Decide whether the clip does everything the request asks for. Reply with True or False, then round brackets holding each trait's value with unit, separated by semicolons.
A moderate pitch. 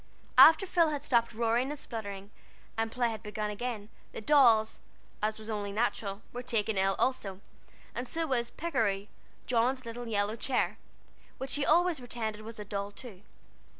False (230 Hz)